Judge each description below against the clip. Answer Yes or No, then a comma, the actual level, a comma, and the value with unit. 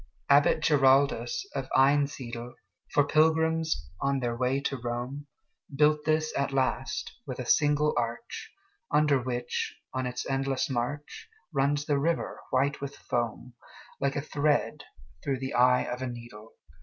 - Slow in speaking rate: Yes, slow, 125 wpm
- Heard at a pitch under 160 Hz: Yes, medium, 140 Hz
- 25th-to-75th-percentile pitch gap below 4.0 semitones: Yes, average, 2.9 semitones